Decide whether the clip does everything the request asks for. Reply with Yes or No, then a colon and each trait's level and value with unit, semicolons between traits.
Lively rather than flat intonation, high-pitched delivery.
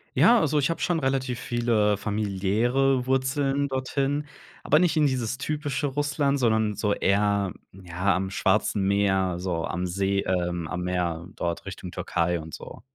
No: wide, 6.3 semitones; low, 105 Hz